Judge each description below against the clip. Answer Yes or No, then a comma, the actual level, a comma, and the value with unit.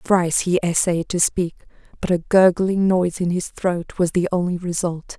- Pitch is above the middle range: No, medium, 175 Hz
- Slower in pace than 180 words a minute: No, average, 185 wpm